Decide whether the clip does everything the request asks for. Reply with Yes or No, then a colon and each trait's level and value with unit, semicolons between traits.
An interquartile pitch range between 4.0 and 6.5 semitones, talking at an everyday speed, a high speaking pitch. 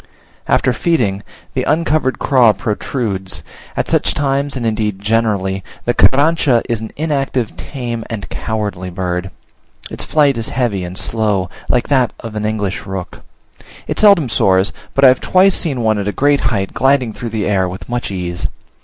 No: average, 5.2 semitones; average, 170 wpm; low, 115 Hz